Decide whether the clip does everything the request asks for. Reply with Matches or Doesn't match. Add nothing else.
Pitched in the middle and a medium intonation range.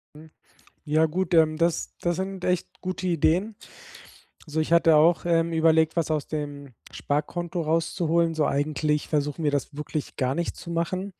Doesn't match